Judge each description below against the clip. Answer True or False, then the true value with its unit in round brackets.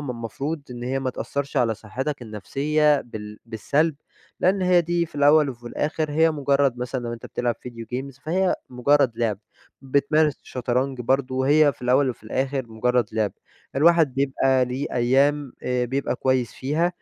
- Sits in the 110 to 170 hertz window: True (135 Hz)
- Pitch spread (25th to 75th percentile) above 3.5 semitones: False (3.2 semitones)